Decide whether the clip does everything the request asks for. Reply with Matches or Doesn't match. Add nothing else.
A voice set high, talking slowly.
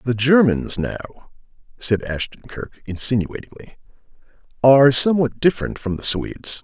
Doesn't match